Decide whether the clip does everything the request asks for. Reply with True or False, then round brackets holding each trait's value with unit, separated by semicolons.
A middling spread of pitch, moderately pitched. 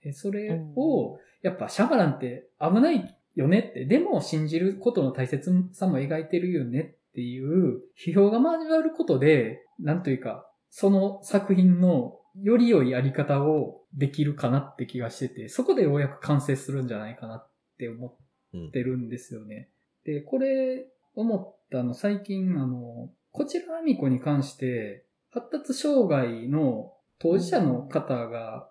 False (7.5 semitones; 150 Hz)